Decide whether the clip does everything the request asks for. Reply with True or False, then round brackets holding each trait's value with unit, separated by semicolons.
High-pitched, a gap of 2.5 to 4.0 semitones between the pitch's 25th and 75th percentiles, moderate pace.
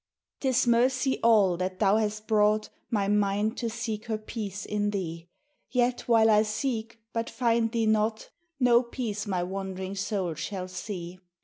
True (215 Hz; 2.8 semitones; 165 wpm)